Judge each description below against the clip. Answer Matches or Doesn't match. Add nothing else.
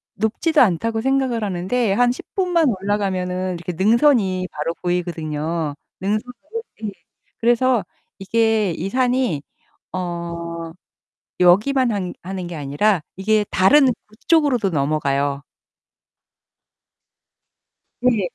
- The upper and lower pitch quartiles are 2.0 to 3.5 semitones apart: Doesn't match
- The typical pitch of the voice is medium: Doesn't match